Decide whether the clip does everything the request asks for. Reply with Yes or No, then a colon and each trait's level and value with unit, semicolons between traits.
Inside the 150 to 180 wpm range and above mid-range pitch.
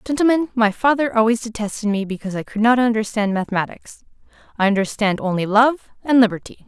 Yes: average, 160 wpm; high, 225 Hz